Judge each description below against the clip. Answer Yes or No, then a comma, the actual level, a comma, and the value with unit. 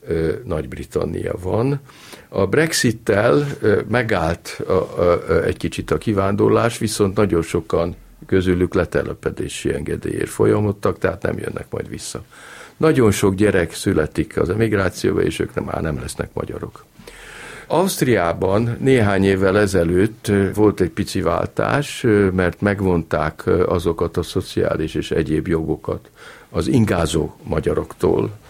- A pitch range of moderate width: Yes, average, 3.1 semitones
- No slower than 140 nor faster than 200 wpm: No, average, 115 wpm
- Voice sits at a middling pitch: No, low, 105 Hz